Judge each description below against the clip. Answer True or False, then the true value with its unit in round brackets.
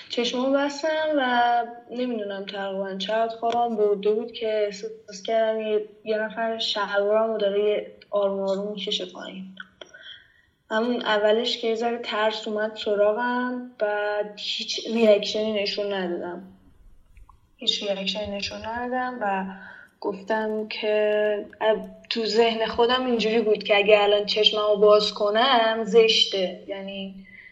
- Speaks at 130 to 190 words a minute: False (120 wpm)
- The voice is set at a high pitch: True (215 Hz)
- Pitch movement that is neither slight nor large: False (1.7 semitones)